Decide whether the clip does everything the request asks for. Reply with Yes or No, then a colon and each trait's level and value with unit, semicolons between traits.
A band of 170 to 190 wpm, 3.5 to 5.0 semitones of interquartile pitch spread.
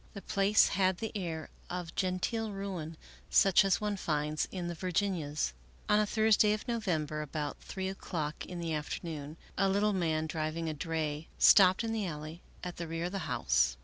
Yes: average, 185 wpm; average, 4.1 semitones